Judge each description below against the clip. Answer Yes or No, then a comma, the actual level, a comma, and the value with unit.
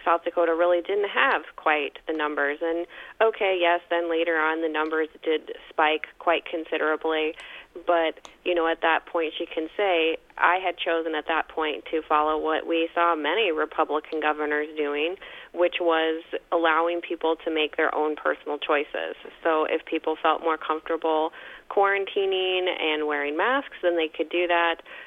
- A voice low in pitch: No, medium, 165 Hz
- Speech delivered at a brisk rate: No, average, 165 wpm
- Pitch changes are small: Yes, narrow, 1.8 semitones